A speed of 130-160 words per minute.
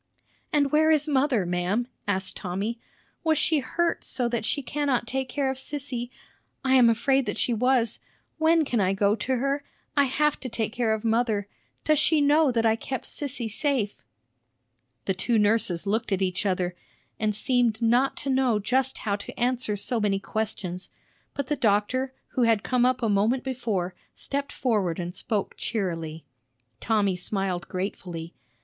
No: average, 170 wpm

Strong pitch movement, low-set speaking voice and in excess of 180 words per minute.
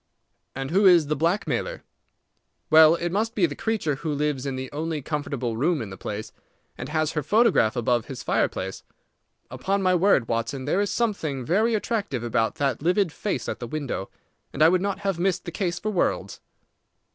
No: wide, 6.2 semitones; medium, 155 Hz; average, 190 wpm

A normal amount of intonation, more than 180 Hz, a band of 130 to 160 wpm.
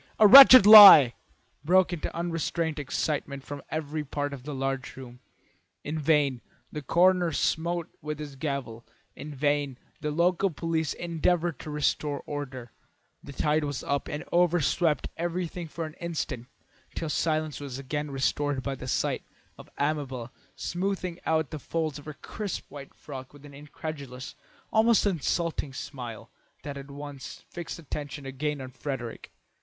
No: average, 3.3 semitones; medium, 150 Hz; average, 150 wpm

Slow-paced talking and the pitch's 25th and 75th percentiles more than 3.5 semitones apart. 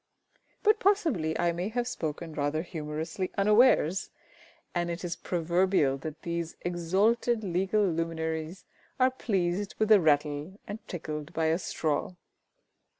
Yes: slow, 130 wpm; average, 4.1 semitones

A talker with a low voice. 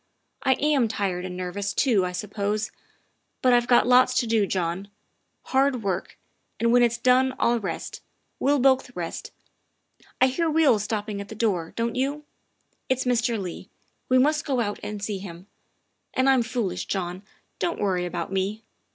No: high, 225 Hz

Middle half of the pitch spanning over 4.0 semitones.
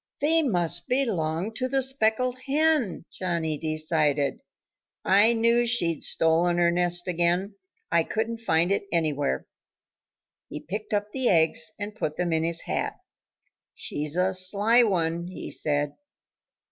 Yes: wide, 5.6 semitones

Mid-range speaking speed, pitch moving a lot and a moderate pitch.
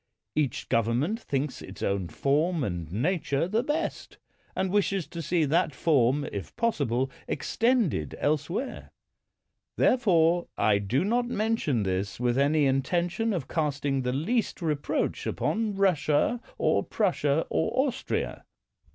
No: slow, 125 wpm; wide, 6.9 semitones; medium, 155 Hz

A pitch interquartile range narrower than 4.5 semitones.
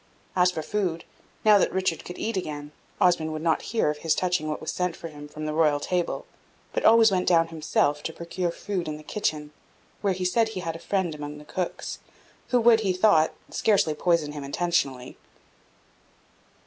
Yes: average, 3.4 semitones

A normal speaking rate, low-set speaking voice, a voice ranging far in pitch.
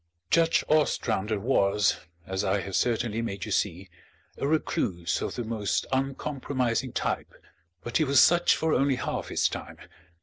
Yes: average, 155 wpm; low, 120 Hz; wide, 5.7 semitones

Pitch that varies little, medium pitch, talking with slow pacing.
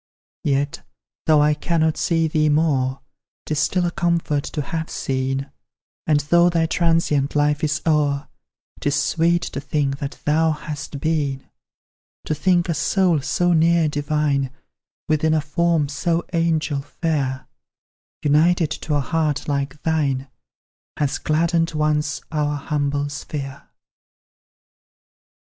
Yes: narrow, 2.3 semitones; medium, 150 Hz; slow, 125 wpm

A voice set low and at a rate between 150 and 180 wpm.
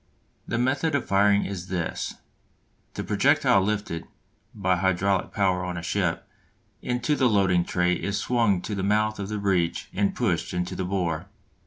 Yes: low, 100 Hz; average, 165 wpm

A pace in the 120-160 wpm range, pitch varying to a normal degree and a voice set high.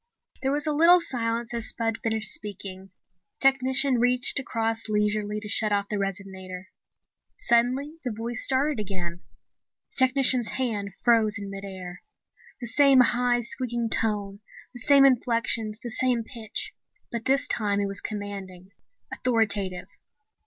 Yes: average, 145 wpm; average, 3.8 semitones; high, 225 Hz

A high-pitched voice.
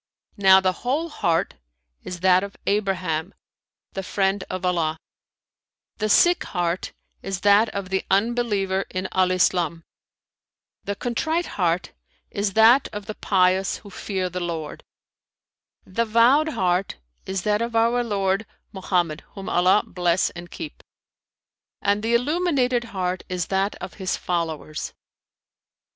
Yes: high, 195 Hz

